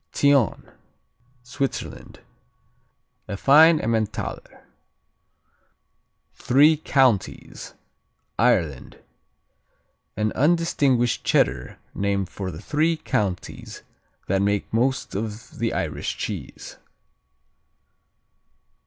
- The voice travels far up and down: Yes, wide, 6.2 semitones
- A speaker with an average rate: No, slow, 75 wpm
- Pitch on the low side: Yes, low, 115 Hz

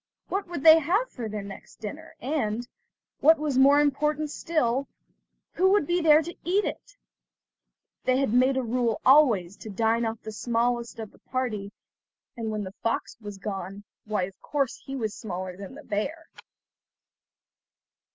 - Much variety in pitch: Yes, wide, 5.9 semitones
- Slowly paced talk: No, average, 165 wpm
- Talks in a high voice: Yes, very high, 250 Hz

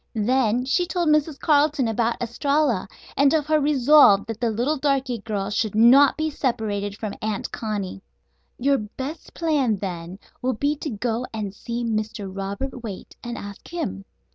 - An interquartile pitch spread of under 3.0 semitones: No, average, 5.1 semitones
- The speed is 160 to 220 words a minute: Yes, average, 165 wpm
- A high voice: Yes, high, 240 Hz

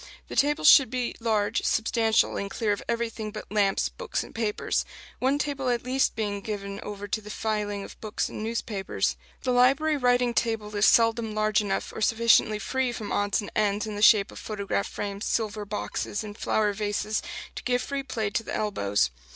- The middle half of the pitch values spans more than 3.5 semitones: No, narrow, 2.4 semitones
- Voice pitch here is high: Yes, high, 215 Hz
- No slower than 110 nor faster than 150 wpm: No, average, 190 wpm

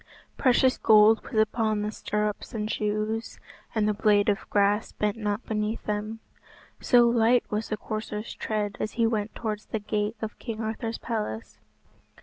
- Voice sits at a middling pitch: No, high, 215 Hz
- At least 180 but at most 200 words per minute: No, average, 160 wpm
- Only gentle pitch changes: Yes, narrow, 1.2 semitones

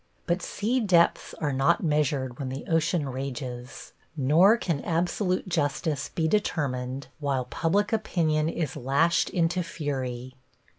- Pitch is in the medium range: Yes, medium, 155 Hz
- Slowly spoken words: Yes, slow, 130 wpm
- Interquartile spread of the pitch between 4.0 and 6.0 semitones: Yes, average, 4.3 semitones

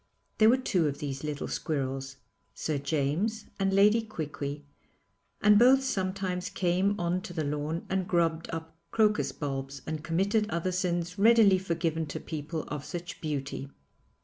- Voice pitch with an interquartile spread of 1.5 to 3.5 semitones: No, average, 4.7 semitones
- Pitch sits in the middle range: Yes, medium, 170 Hz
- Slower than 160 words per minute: Yes, average, 150 wpm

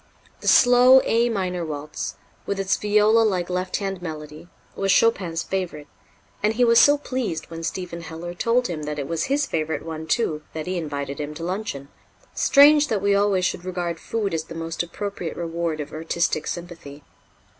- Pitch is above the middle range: No, medium, 175 Hz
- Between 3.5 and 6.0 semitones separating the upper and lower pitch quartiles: Yes, average, 4.4 semitones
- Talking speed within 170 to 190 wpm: Yes, average, 180 wpm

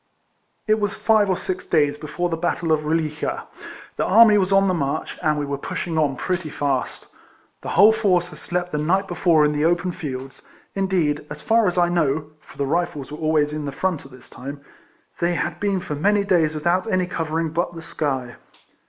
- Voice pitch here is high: No, medium, 165 Hz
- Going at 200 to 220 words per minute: Yes, fast, 205 wpm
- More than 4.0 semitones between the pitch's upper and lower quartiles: No, average, 3.7 semitones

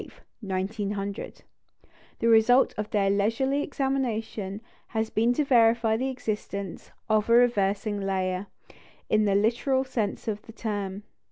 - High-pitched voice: Yes, high, 215 Hz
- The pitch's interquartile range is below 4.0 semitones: Yes, average, 2.8 semitones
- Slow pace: Yes, slow, 120 wpm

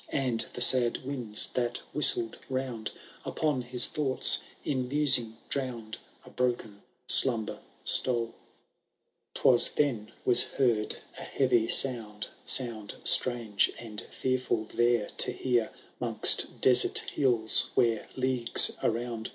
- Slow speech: Yes, slow, 120 wpm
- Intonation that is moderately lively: No, narrow, 2.3 semitones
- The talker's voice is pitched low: Yes, low, 120 Hz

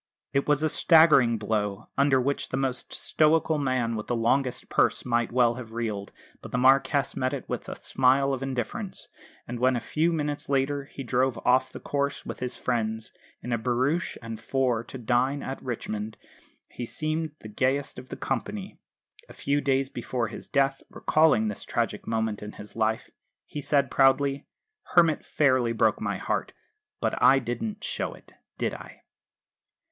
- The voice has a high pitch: No, low, 130 Hz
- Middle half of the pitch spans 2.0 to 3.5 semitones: Yes, average, 3.1 semitones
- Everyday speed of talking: Yes, average, 175 wpm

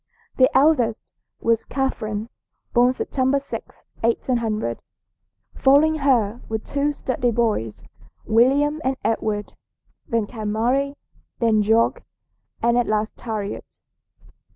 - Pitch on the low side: No, high, 235 Hz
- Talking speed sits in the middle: No, slow, 105 wpm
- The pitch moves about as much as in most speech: Yes, average, 3.6 semitones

